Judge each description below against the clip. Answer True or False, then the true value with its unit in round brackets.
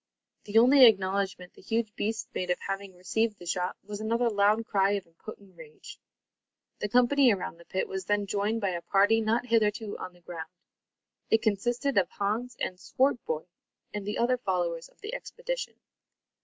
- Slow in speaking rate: False (175 wpm)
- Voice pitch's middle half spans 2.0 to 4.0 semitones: True (3.5 semitones)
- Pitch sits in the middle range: False (205 Hz)